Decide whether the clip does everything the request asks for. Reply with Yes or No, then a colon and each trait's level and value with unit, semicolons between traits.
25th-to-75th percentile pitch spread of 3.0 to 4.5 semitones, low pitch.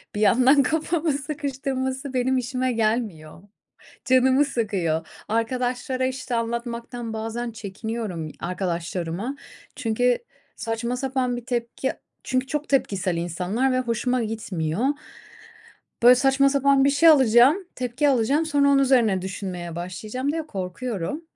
No: average, 3.9 semitones; high, 245 Hz